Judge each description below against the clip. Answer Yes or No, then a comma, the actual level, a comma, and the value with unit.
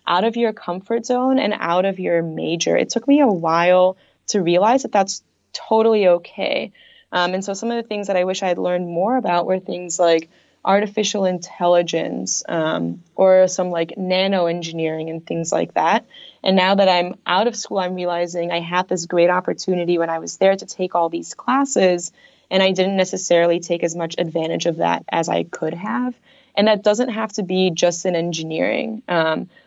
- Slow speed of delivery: No, average, 200 wpm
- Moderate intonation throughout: Yes, average, 3.4 semitones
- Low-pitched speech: No, medium, 185 Hz